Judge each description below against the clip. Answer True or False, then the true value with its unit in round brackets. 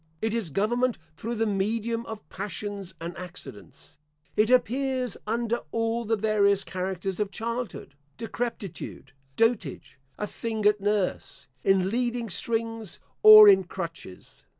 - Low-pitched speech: False (215 Hz)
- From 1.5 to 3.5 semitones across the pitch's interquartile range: True (3.1 semitones)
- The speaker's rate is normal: False (125 wpm)